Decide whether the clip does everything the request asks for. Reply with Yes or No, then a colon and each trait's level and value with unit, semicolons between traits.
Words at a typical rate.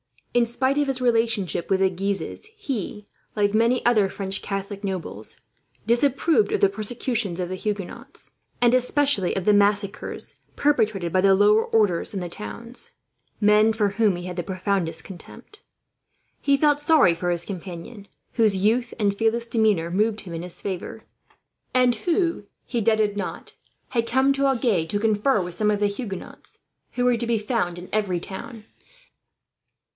Yes: average, 165 wpm